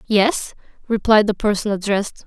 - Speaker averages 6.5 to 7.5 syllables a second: No, 5.1 syllables/s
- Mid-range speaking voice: No, high, 210 Hz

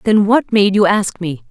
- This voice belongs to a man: No, female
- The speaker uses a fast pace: Yes, fast, 240 wpm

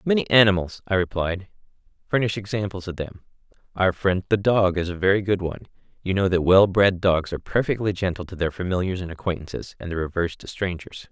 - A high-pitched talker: No, very low, 95 Hz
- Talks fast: No, average, 195 wpm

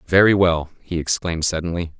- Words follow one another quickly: No, average, 150 wpm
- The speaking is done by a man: Yes, male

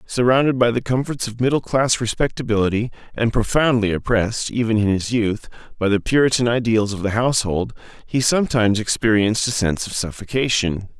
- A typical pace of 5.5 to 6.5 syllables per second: Yes, 5.8 syllables/s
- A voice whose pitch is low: Yes, low, 115 Hz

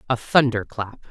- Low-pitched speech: Yes, low, 120 Hz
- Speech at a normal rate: Yes, average, 165 wpm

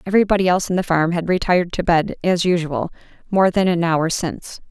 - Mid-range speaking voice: Yes, medium, 175 Hz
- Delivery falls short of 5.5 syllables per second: No, 6.2 syllables/s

